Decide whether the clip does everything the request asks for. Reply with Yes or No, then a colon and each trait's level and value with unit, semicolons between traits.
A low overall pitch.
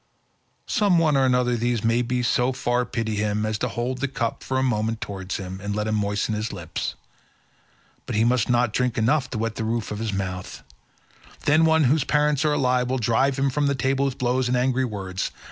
Yes: low, 120 Hz